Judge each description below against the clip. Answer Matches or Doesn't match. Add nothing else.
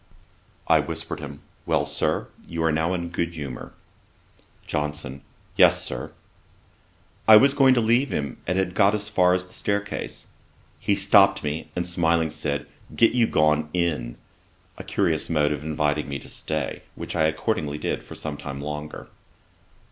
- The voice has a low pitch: Matches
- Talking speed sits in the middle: Matches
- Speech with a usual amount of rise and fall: Matches